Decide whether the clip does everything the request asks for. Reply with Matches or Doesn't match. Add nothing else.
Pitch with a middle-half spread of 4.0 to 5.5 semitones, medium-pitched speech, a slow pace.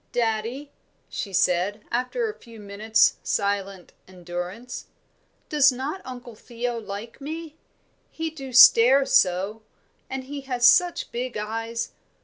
Doesn't match